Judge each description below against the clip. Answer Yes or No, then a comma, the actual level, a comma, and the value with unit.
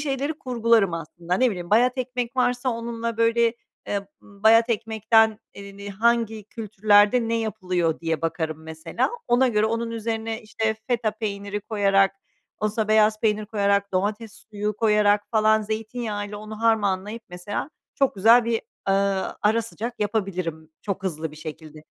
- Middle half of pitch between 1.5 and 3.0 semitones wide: Yes, narrow, 2.5 semitones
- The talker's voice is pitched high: Yes, high, 215 Hz